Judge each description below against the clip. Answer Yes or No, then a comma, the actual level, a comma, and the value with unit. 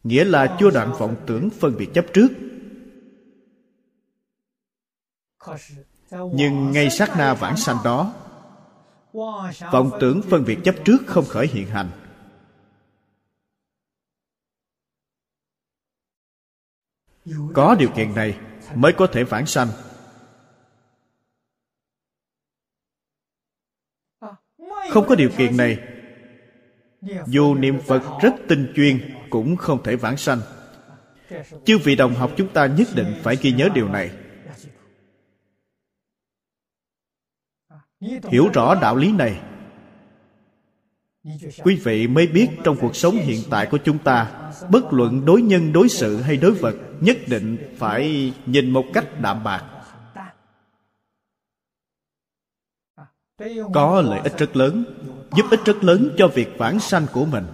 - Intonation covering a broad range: Yes, wide, 7.2 semitones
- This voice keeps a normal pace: No, slow, 120 wpm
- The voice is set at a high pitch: No, medium, 140 Hz